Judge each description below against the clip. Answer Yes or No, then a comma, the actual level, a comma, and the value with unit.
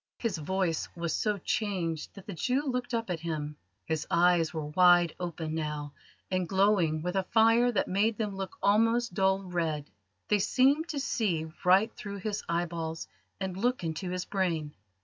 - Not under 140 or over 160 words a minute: No, average, 170 wpm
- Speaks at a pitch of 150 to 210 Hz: Yes, medium, 185 Hz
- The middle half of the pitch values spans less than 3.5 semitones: No, average, 4.4 semitones